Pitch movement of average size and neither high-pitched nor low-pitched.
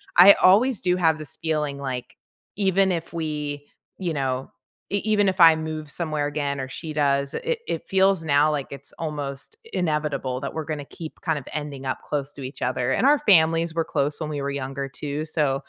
Yes: average, 3.1 semitones; medium, 150 Hz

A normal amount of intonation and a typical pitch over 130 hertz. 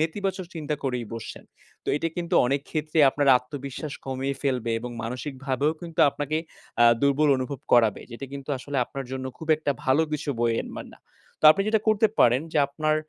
Yes: average, 3.1 semitones; medium, 140 Hz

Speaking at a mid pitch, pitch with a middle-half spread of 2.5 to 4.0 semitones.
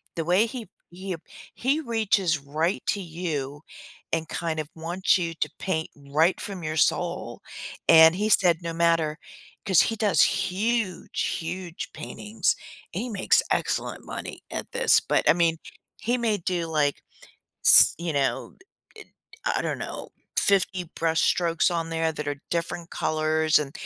Yes: medium, 170 Hz; average, 3.4 semitones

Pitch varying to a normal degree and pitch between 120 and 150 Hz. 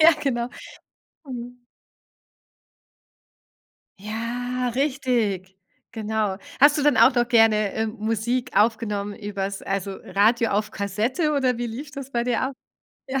No: average, 3.3 semitones; high, 230 Hz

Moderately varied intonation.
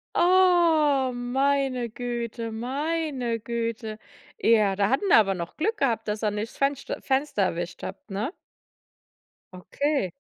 Yes: average, 4.7 semitones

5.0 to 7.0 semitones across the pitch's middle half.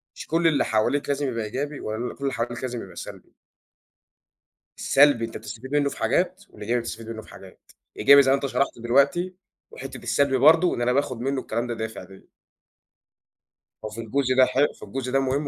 No: average, 3.5 semitones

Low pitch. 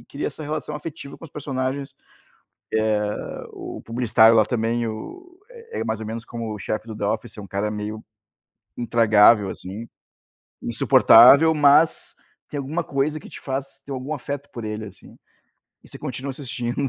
Yes: low, 125 Hz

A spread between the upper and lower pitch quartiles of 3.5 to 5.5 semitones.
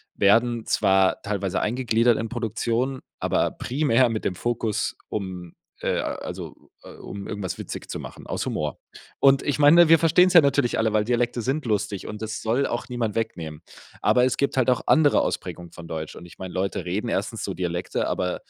Yes: average, 4.7 semitones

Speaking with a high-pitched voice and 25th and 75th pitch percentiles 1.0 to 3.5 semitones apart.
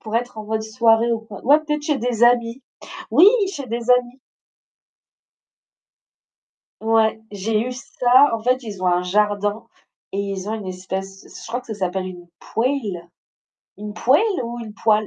Yes: high, 225 Hz; average, 3.2 semitones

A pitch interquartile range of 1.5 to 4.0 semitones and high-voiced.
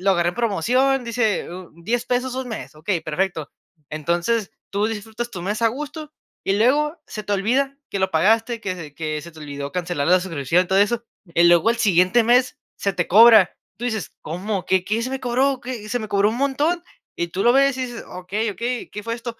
No: average, 5.1 semitones; high, 215 Hz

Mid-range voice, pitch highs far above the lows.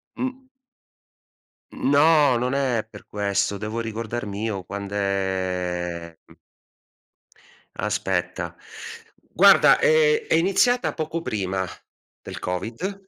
No: low, 110 Hz; wide, 9.0 semitones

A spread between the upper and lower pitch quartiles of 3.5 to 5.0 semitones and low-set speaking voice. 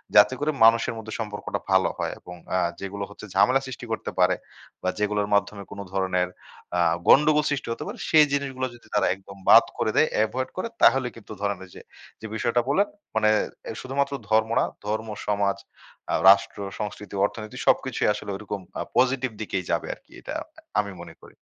Yes: average, 4.4 semitones; low, 110 Hz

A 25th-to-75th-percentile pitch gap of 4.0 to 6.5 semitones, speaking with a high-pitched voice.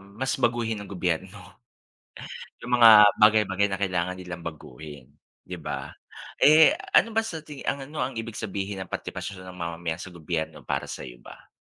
No: average, 5.1 semitones; very low, 95 Hz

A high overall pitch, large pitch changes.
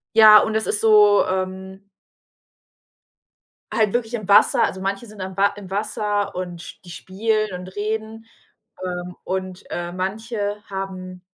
No: high, 200 Hz; narrow, 2.4 semitones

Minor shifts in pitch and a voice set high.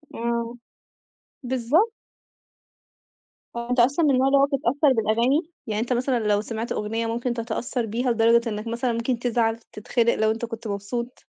Yes: narrow, 1.8 semitones; high, 235 Hz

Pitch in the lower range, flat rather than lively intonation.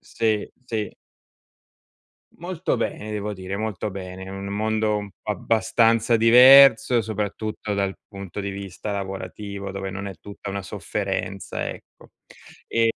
Yes: low, 105 Hz; narrow, 2.1 semitones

